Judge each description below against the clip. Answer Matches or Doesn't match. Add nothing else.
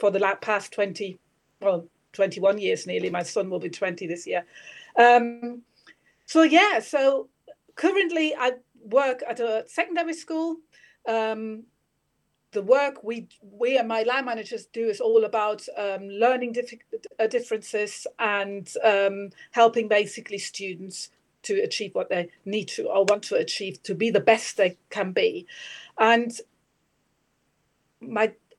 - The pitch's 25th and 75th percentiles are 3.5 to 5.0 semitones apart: Matches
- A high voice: Matches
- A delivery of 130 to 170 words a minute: Matches